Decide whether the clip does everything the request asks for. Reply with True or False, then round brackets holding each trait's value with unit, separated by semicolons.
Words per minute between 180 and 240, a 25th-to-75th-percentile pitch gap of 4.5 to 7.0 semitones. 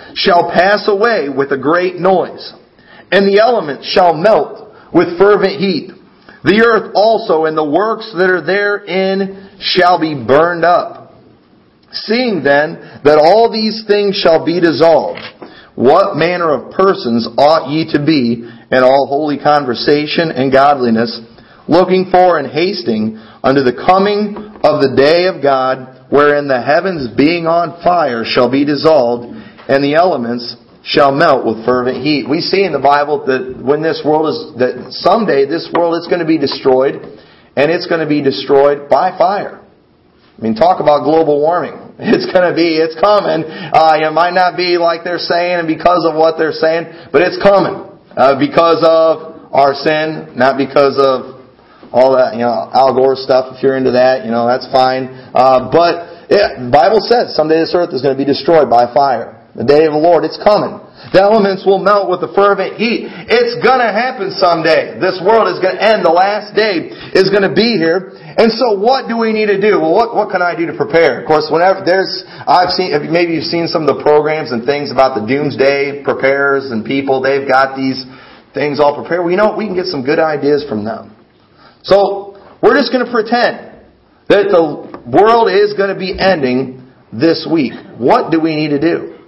True (190 wpm; 5.6 semitones)